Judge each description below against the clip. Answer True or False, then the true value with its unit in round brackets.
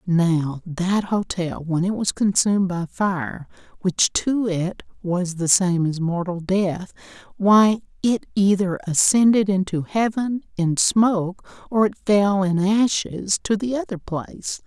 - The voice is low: False (190 Hz)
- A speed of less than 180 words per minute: True (140 wpm)